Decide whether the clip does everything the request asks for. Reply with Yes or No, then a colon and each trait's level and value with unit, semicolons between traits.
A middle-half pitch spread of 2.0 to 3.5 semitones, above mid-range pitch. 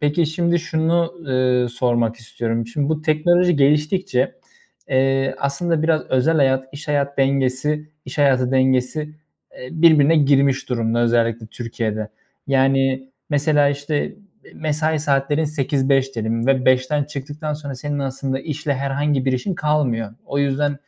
No: average, 2.7 semitones; medium, 140 Hz